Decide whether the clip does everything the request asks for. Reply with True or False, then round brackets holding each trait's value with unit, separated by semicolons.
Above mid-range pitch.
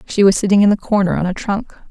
True (195 Hz)